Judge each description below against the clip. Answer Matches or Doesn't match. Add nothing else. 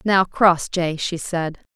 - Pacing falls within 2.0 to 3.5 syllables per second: Matches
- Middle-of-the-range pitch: Matches